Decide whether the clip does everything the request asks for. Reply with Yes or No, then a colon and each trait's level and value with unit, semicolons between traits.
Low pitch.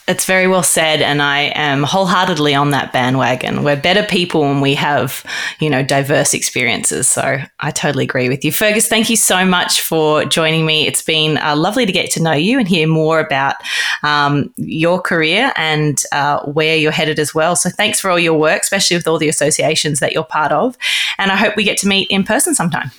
No: medium, 160 Hz